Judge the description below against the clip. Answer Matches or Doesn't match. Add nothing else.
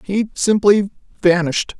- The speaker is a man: Doesn't match